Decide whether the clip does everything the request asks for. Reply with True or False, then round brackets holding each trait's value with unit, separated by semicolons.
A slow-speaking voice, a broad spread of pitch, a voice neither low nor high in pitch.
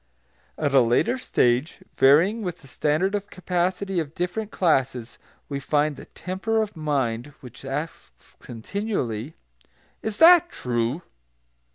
True (130 wpm; 6.6 semitones; 155 Hz)